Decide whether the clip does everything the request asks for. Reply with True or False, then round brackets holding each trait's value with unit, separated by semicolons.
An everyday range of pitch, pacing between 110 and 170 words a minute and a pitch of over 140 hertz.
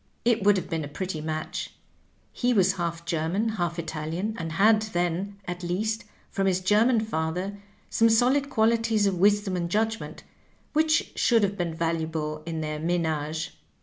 True (4.8 semitones; 160 wpm; 185 Hz)